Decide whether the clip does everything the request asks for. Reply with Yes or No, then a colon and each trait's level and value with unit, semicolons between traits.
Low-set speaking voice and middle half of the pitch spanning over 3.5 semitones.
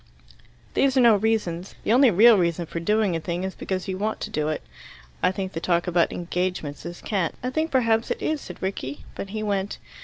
No: high, 190 Hz; average, 4.3 semitones